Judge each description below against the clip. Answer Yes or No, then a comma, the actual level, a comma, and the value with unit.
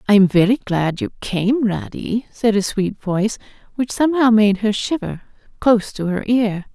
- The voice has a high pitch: Yes, high, 210 Hz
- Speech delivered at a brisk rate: No, average, 170 wpm